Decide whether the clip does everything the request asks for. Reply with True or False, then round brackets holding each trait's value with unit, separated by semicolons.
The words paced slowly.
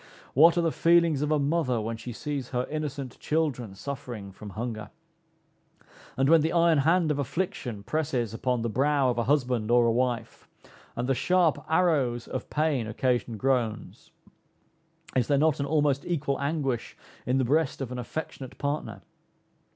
False (165 wpm)